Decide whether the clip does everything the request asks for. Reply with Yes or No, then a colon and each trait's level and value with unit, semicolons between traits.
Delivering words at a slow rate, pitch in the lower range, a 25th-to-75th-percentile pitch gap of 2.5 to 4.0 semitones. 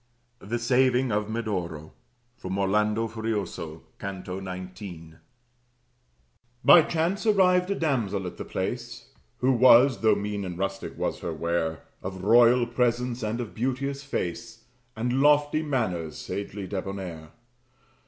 No: slow, 125 wpm; low, 110 Hz; average, 5.0 semitones